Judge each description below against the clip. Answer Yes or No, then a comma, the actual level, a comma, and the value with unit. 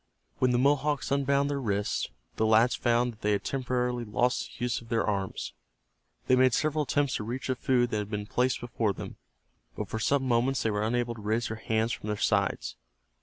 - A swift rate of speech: Yes, fast, 215 wpm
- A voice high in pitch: No, low, 120 Hz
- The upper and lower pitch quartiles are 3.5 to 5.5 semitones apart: No, average, 2.9 semitones